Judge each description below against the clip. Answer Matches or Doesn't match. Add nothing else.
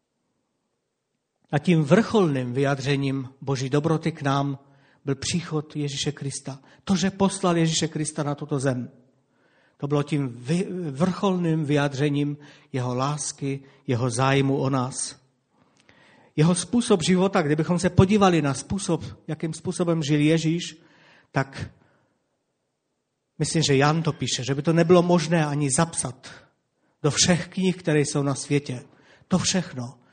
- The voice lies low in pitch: Doesn't match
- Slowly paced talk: Doesn't match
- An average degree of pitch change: Matches